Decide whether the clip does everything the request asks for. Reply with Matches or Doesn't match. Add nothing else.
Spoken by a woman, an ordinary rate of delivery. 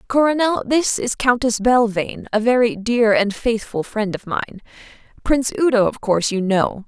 Matches